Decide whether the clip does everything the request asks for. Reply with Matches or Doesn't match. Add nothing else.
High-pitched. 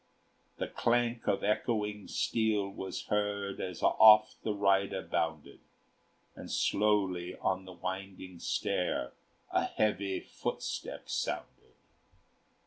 Doesn't match